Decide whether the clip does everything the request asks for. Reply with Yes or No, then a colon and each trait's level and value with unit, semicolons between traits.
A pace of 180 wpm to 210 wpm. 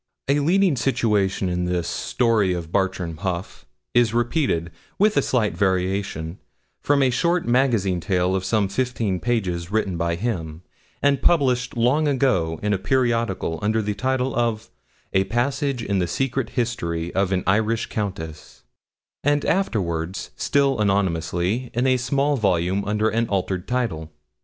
No: average, 145 wpm